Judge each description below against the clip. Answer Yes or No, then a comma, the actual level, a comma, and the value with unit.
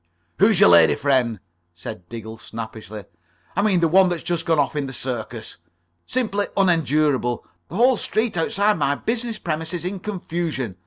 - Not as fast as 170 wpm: Yes, average, 160 wpm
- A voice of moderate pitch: Yes, medium, 160 Hz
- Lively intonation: Yes, wide, 8.2 semitones